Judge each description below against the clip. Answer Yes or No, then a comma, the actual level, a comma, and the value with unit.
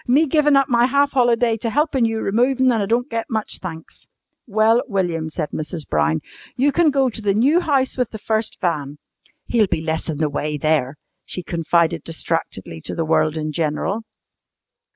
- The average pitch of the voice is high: Yes, high, 215 Hz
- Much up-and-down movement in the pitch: Yes, wide, 7.8 semitones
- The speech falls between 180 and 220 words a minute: Yes, average, 190 wpm